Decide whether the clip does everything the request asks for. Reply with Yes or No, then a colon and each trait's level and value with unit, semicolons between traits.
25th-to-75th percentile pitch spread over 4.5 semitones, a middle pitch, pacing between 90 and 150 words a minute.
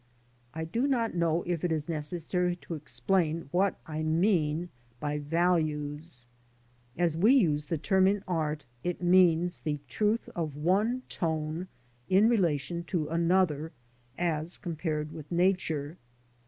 No: average, 2.9 semitones; medium, 165 Hz; average, 140 wpm